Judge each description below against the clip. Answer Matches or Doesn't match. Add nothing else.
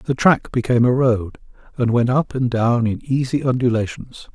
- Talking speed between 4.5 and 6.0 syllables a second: Matches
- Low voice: Matches